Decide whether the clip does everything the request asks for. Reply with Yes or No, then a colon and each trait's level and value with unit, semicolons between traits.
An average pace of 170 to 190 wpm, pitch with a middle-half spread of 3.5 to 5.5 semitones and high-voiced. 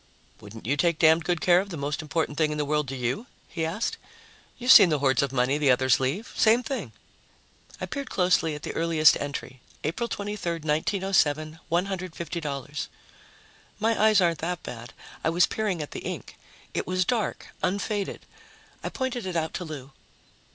No: average, 180 wpm; average, 4.7 semitones; medium, 165 Hz